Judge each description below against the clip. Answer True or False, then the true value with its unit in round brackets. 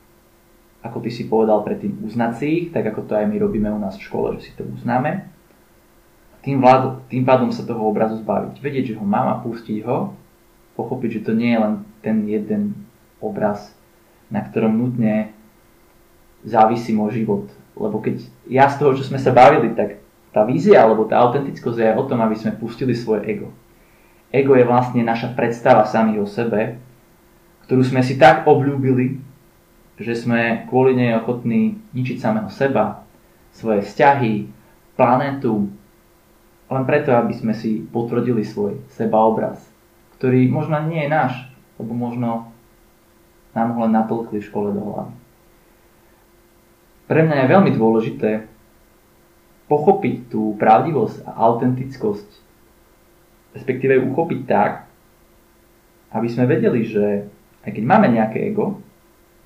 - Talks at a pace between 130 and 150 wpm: True (145 wpm)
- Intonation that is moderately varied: True (3.1 semitones)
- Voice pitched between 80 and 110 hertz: False (120 Hz)